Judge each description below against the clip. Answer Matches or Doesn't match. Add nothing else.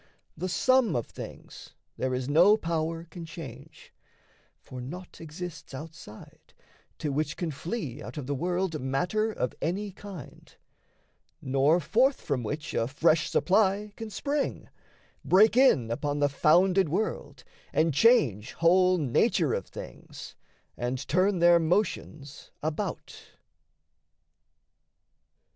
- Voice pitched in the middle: Matches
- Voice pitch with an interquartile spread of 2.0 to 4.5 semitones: Doesn't match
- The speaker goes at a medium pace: Doesn't match